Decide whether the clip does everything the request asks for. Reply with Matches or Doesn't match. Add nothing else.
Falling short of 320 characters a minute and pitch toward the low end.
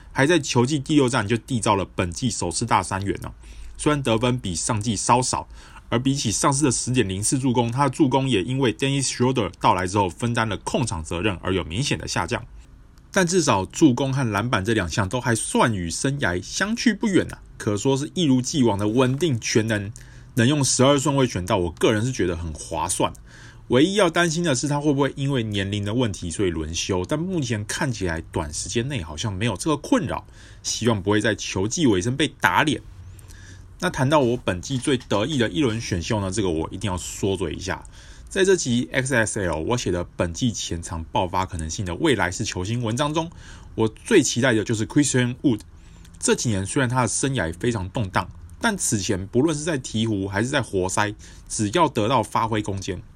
Doesn't match